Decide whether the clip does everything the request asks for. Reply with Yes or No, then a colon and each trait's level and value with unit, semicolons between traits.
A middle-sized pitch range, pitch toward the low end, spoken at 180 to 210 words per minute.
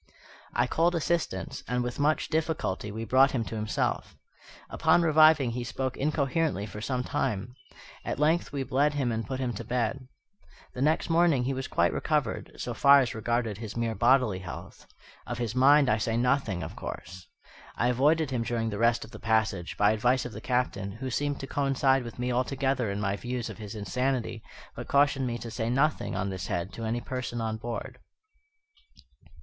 Yes: average, 3.6 semitones; low, 125 Hz; average, 190 wpm